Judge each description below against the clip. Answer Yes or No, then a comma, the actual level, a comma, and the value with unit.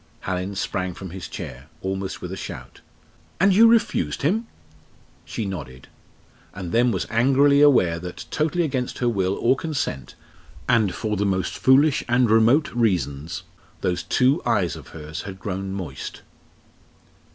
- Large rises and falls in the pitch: Yes, wide, 6.3 semitones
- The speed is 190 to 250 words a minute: No, average, 150 wpm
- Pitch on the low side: Yes, low, 100 Hz